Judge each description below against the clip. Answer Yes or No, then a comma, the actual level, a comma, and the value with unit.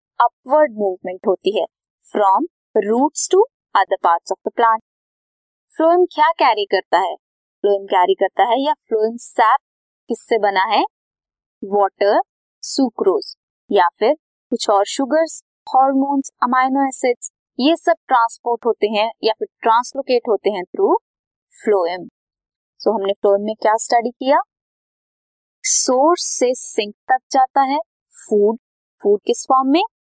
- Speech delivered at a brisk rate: No, average, 130 wpm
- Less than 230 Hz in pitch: No, very high, 250 Hz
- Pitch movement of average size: No, wide, 6.9 semitones